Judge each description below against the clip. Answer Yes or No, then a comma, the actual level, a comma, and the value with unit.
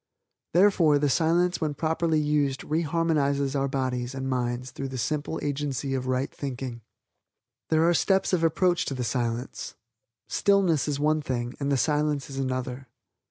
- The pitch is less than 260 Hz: Yes, medium, 140 Hz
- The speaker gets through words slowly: No, average, 160 wpm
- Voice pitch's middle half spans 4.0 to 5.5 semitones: No, average, 3.4 semitones